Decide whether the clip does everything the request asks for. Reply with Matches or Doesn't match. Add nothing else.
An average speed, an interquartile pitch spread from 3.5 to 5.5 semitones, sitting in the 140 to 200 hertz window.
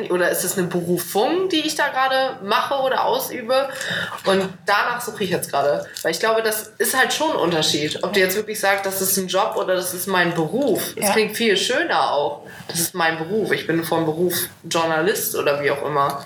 Doesn't match